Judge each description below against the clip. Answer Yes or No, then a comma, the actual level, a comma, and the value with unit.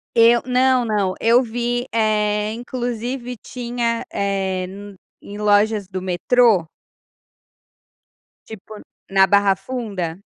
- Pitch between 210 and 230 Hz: Yes, high, 215 Hz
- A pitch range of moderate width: Yes, average, 3.4 semitones